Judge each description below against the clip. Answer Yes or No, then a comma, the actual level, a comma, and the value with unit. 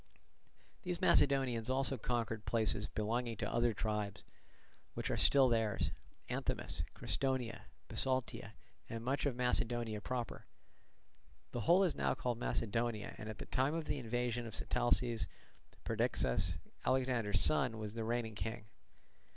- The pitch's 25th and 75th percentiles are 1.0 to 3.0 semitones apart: Yes, average, 2.7 semitones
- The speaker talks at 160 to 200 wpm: No, slow, 135 wpm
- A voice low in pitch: Yes, low, 120 Hz